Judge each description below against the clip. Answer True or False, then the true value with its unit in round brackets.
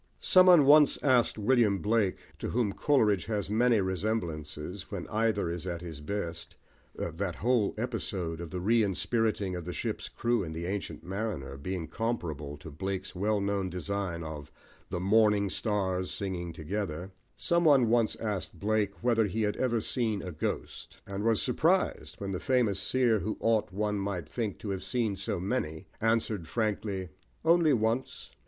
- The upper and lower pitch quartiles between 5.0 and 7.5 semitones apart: False (4.1 semitones)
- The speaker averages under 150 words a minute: False (155 wpm)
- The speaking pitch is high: False (100 Hz)